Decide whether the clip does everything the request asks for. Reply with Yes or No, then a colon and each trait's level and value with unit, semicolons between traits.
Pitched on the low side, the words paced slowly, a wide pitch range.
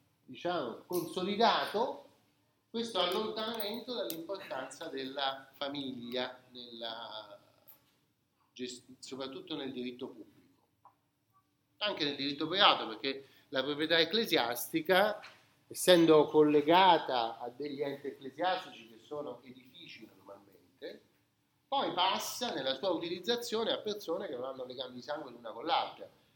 No: medium, 145 Hz; slow, 105 wpm; wide, 5.7 semitones